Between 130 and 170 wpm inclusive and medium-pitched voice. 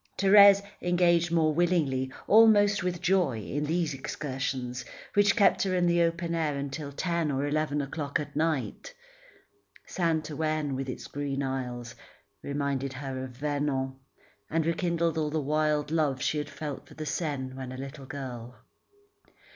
Yes: average, 155 wpm; medium, 150 Hz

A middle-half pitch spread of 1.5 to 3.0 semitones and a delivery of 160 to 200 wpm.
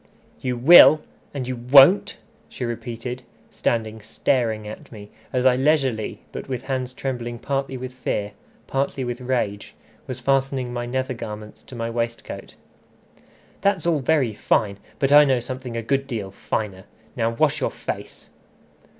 No: average, 2.7 semitones; average, 150 wpm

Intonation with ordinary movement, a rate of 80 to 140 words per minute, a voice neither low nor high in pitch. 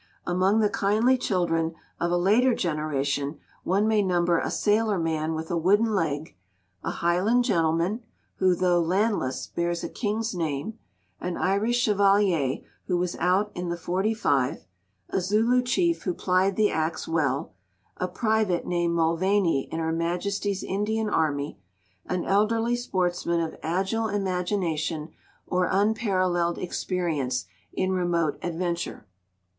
Yes: average, 3.8 semitones; slow, 135 wpm; medium, 180 Hz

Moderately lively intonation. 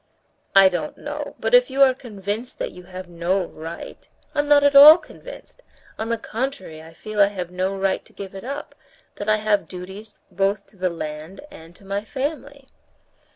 No: wide, 6.5 semitones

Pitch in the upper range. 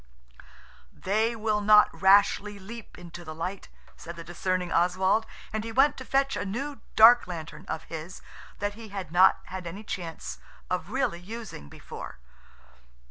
Yes: high, 195 Hz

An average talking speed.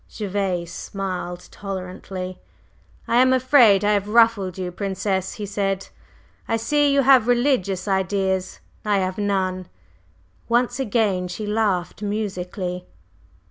No: slow, 120 wpm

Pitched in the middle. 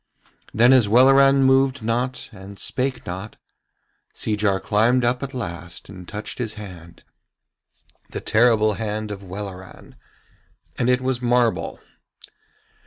No: low, 110 Hz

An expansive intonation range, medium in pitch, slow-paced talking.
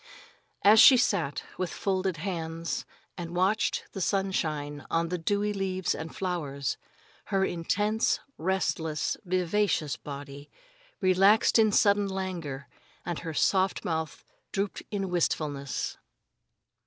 No: average, 3.5 semitones; medium, 180 Hz; slow, 115 wpm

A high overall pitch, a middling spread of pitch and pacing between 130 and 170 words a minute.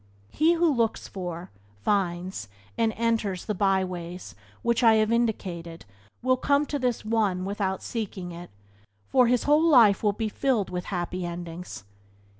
Yes: high, 205 Hz; average, 4.6 semitones; average, 150 wpm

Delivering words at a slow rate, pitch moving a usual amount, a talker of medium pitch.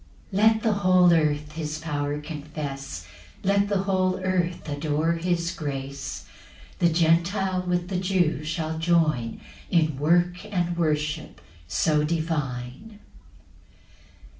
Yes: slow, 115 wpm; average, 3.3 semitones; medium, 165 Hz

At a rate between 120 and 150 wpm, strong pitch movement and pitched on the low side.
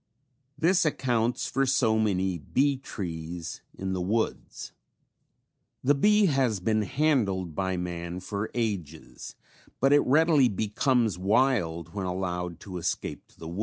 Yes: slow, 135 wpm; wide, 6.7 semitones; low, 105 Hz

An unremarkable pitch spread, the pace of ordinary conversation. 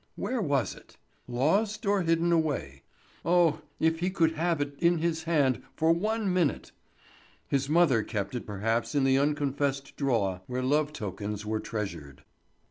No: wide, 5.9 semitones; average, 160 wpm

